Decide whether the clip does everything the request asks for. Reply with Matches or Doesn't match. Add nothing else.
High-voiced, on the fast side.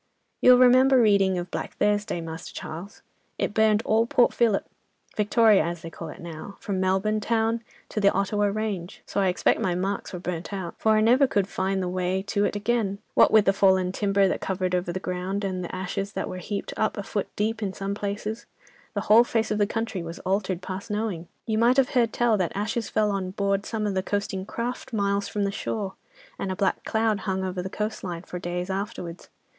Matches